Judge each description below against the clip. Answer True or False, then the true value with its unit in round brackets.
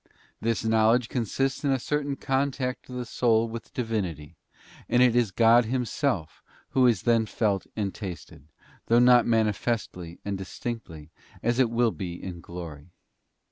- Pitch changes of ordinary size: True (4.2 semitones)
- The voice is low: True (115 Hz)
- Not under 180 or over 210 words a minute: False (155 wpm)